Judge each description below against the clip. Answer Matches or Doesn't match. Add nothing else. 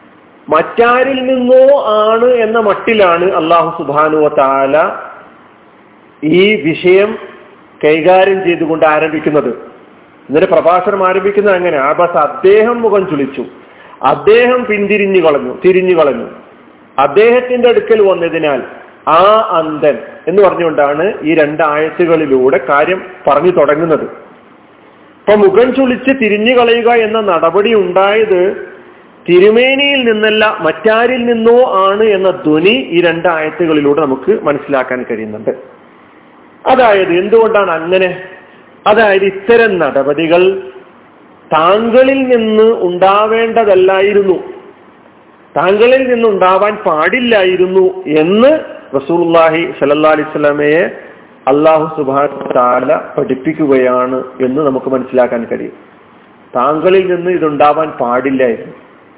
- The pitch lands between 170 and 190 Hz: Matches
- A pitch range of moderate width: Doesn't match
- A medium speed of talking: Matches